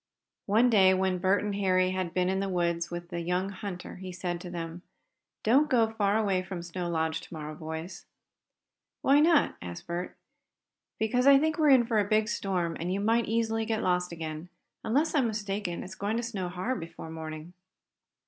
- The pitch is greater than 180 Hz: Yes, high, 190 Hz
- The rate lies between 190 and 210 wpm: Yes, average, 195 wpm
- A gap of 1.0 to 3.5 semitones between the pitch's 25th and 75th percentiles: No, average, 4.2 semitones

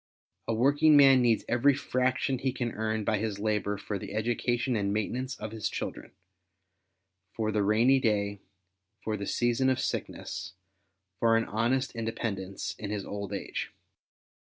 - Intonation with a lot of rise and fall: No, average, 3.5 semitones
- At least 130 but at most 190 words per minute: Yes, average, 160 wpm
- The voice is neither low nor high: No, low, 115 Hz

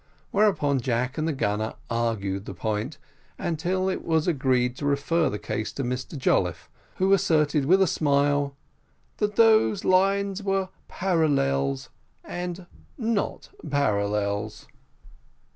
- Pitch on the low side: No, medium, 145 Hz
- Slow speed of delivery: Yes, slow, 125 wpm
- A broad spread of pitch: Yes, wide, 8.0 semitones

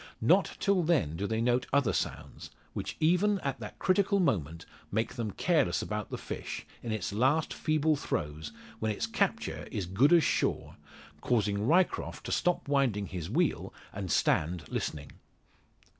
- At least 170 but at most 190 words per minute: No, average, 160 wpm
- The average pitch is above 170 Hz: No, low, 115 Hz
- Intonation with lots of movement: Yes, wide, 8.0 semitones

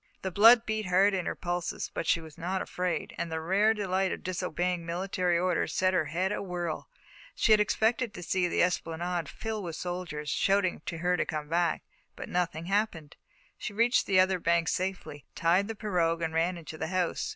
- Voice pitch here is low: No, medium, 180 Hz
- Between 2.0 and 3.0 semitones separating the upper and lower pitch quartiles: Yes, narrow, 2.4 semitones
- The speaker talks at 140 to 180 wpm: No, average, 195 wpm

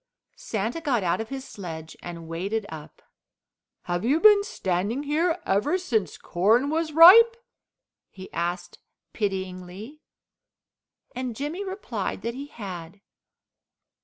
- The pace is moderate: No, slow, 120 wpm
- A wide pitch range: Yes, wide, 8.5 semitones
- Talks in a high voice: Yes, high, 220 Hz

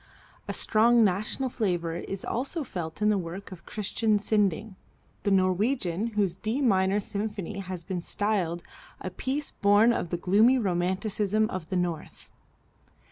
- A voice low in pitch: No, high, 200 Hz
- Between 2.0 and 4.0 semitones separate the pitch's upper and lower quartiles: Yes, average, 3.2 semitones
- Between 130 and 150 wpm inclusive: Yes, average, 145 wpm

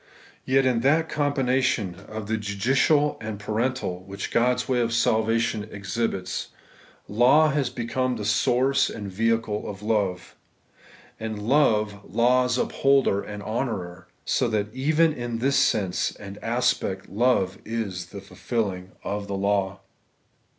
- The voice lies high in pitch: No, low, 115 Hz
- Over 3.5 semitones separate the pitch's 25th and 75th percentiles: Yes, average, 3.9 semitones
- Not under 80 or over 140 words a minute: Yes, slow, 135 wpm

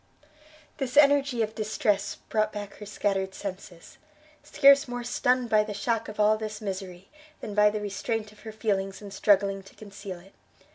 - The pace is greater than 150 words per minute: Yes, average, 175 wpm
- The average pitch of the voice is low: No, high, 210 Hz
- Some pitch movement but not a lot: No, narrow, 2.2 semitones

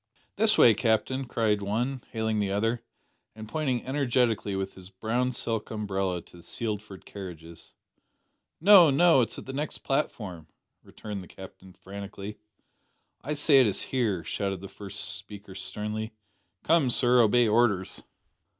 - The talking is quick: No, average, 145 wpm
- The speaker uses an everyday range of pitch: Yes, average, 4.3 semitones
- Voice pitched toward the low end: Yes, low, 110 Hz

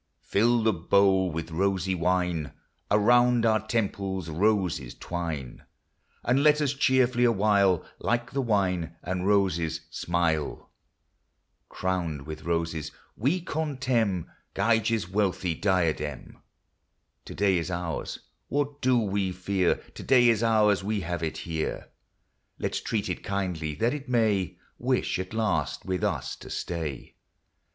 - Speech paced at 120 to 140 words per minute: Yes, slow, 135 wpm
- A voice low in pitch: Yes, very low, 95 Hz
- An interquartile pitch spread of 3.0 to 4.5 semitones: No, average, 5.1 semitones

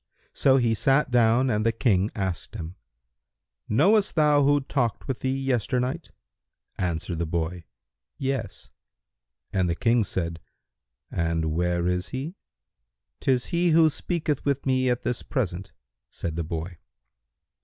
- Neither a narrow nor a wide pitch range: No, wide, 7.4 semitones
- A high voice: No, low, 115 Hz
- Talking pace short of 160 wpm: Yes, slow, 135 wpm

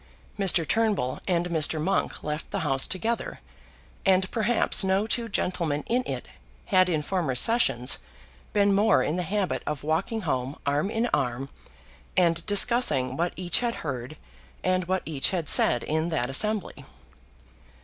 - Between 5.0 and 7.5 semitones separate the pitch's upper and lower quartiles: Yes, average, 5.3 semitones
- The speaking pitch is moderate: Yes, medium, 175 Hz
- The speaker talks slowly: No, average, 150 wpm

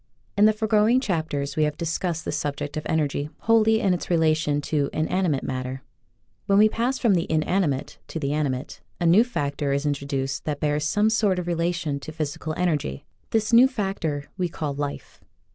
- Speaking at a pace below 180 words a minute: No, average, 185 wpm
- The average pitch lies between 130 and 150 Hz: No, medium, 160 Hz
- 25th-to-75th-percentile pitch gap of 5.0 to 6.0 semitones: Yes, wide, 5.4 semitones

